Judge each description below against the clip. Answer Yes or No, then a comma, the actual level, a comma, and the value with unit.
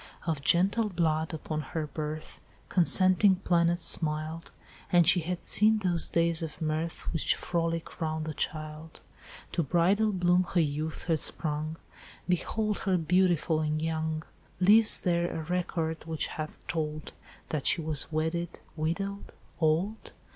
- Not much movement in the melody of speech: Yes, narrow, 2.3 semitones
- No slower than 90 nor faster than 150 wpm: Yes, average, 140 wpm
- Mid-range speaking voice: Yes, medium, 165 Hz